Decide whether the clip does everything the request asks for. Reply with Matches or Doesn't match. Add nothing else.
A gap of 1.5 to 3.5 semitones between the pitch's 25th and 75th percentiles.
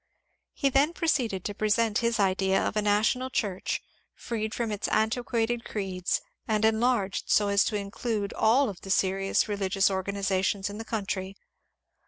Matches